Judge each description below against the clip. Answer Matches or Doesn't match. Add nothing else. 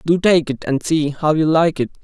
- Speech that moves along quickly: Matches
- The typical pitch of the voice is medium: Matches